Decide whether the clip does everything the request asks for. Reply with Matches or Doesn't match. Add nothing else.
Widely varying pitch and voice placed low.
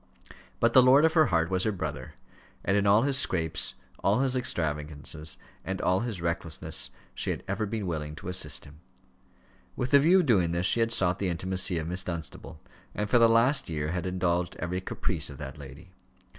Matches